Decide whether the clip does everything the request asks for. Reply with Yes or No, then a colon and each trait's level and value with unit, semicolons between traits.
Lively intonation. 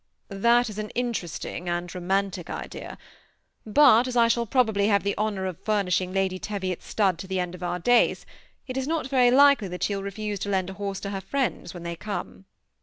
No: average, 4.1 semitones